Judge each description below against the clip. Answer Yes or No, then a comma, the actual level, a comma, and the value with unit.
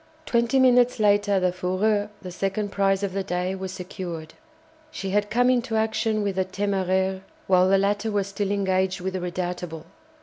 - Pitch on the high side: Yes, high, 195 Hz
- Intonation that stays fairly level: Yes, narrow, 1.9 semitones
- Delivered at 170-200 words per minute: Yes, average, 175 wpm